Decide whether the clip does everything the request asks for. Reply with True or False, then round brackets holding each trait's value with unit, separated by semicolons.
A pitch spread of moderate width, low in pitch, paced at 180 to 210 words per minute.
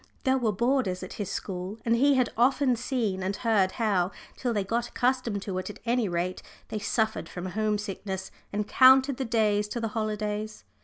False (3.6 semitones; 215 Hz; 195 wpm)